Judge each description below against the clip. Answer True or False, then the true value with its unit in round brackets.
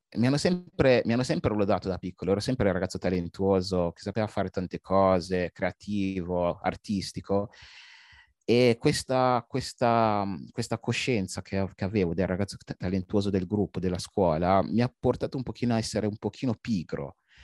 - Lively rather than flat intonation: False (4.3 semitones)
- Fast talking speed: False (155 wpm)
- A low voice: True (100 Hz)